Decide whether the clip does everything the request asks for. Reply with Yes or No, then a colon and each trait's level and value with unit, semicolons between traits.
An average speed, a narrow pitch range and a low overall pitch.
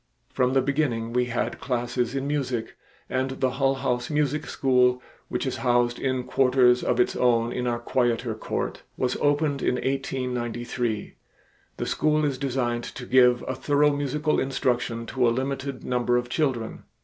Yes: average, 160 wpm; narrow, 1.8 semitones; low, 125 Hz